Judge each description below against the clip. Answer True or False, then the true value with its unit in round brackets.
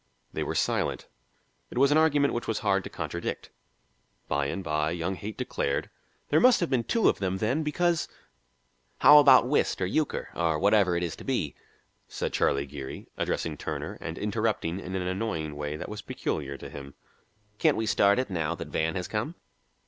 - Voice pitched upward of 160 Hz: False (95 Hz)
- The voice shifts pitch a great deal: True (7.7 semitones)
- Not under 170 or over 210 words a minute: True (195 wpm)